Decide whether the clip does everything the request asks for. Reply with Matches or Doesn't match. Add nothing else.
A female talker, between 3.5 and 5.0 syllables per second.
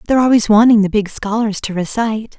Doesn't match